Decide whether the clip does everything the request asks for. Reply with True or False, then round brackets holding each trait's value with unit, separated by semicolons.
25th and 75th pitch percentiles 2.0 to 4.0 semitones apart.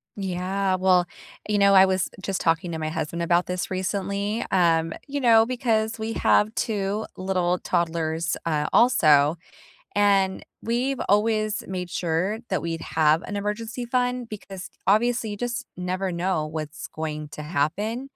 False (4.4 semitones)